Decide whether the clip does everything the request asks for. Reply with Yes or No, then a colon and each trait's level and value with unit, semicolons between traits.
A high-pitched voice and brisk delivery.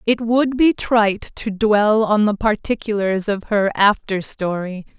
No: high, 210 Hz; average, 155 wpm